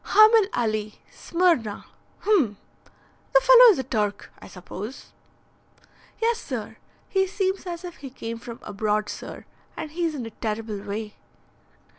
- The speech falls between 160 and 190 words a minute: No, average, 140 wpm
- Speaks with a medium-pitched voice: No, very high, 250 Hz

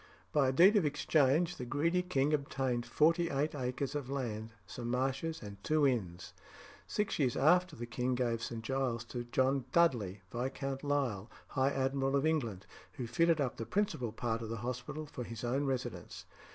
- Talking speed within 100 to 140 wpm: No, average, 180 wpm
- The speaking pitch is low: Yes, low, 130 Hz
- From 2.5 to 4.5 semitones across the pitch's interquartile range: Yes, average, 3.6 semitones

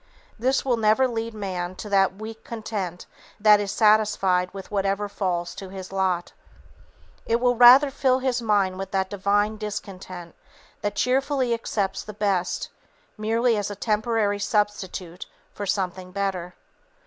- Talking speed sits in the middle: Yes, average, 145 wpm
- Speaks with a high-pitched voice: Yes, high, 205 Hz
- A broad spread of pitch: No, average, 2.8 semitones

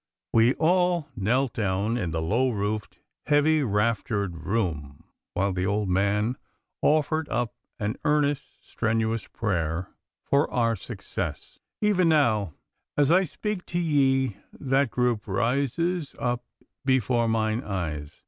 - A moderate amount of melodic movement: No, wide, 5.9 semitones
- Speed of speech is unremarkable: No, slow, 125 wpm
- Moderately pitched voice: No, low, 115 Hz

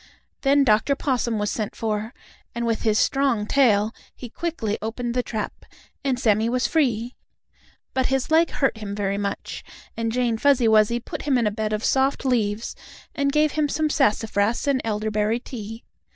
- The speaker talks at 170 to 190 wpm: Yes, average, 175 wpm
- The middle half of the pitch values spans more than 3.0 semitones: Yes, average, 4.0 semitones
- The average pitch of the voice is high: Yes, high, 235 Hz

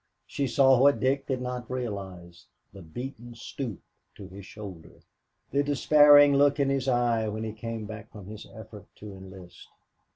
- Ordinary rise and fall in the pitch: Yes, average, 4.8 semitones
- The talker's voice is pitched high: No, low, 115 Hz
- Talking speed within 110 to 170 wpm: Yes, average, 165 wpm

